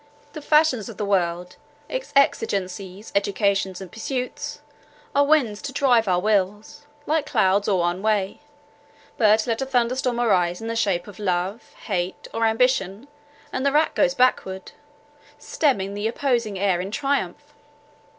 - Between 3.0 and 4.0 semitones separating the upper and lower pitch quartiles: No, average, 4.9 semitones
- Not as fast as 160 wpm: Yes, average, 150 wpm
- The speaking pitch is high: Yes, high, 215 Hz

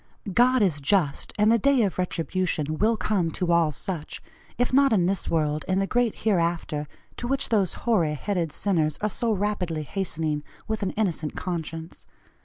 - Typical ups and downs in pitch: Yes, average, 4.9 semitones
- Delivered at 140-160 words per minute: No, average, 175 wpm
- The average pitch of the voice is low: No, medium, 185 Hz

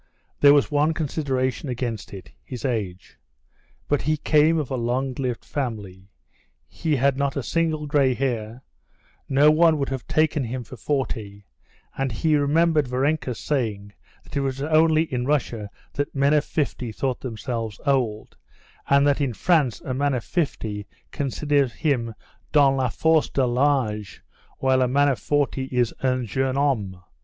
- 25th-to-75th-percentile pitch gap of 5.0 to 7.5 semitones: No, average, 3.4 semitones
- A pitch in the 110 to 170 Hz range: Yes, low, 135 Hz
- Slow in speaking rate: No, average, 160 wpm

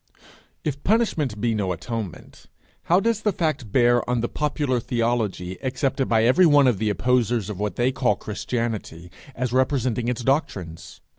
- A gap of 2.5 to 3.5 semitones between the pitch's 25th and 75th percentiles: No, average, 4.0 semitones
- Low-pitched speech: Yes, low, 120 Hz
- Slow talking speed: No, average, 160 wpm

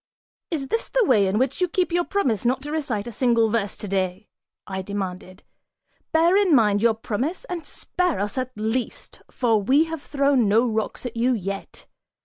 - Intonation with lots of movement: Yes, wide, 6.5 semitones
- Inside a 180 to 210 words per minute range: Yes, average, 185 wpm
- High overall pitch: Yes, high, 240 Hz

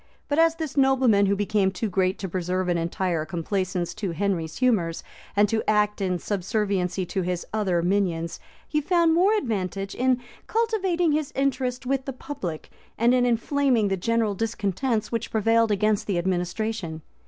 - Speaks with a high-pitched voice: Yes, high, 210 Hz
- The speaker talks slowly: No, average, 165 wpm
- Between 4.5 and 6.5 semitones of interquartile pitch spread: Yes, wide, 5.5 semitones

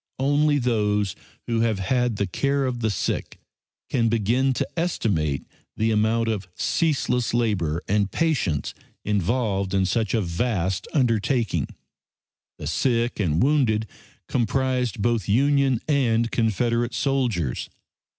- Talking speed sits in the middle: No, slow, 120 wpm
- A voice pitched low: Yes, low, 115 Hz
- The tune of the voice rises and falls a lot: No, average, 4.1 semitones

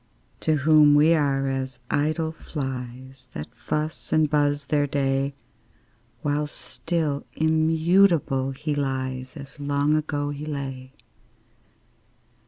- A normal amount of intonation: No, narrow, 2.3 semitones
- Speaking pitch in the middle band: Yes, medium, 145 Hz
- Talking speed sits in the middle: No, slow, 110 wpm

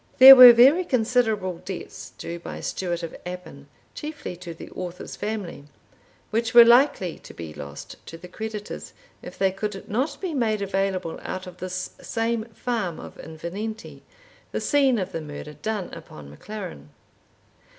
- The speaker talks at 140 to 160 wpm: Yes, average, 155 wpm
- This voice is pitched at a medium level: No, high, 195 Hz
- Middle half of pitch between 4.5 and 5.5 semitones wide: Yes, average, 5.1 semitones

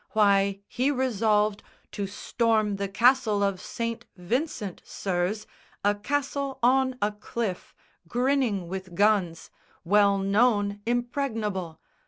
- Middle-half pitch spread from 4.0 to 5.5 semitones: No, average, 3.6 semitones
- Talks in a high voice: Yes, high, 210 Hz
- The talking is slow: Yes, slow, 110 wpm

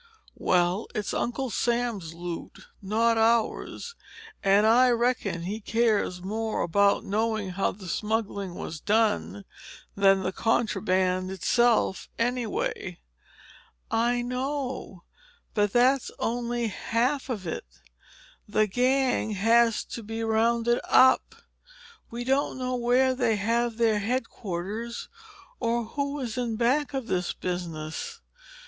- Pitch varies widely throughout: No, average, 3.6 semitones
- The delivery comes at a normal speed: No, slow, 120 wpm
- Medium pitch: No, high, 225 Hz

